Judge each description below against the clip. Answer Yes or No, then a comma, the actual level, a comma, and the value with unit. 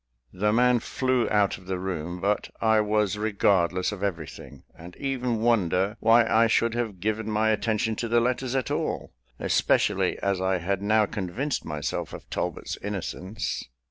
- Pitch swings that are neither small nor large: Yes, average, 3.5 semitones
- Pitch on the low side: Yes, low, 105 Hz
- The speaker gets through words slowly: No, average, 165 wpm